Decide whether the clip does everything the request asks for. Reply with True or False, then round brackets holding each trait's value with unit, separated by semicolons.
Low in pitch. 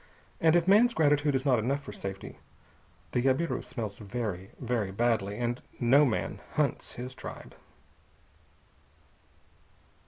True (125 Hz)